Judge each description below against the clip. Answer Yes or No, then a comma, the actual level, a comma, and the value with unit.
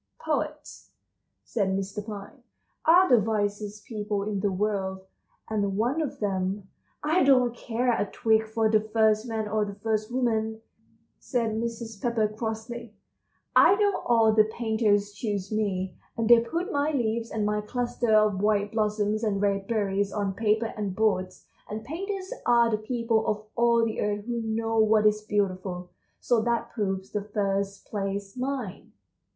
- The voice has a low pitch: No, high, 215 Hz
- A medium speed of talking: Yes, average, 160 wpm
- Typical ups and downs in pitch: No, narrow, 2.3 semitones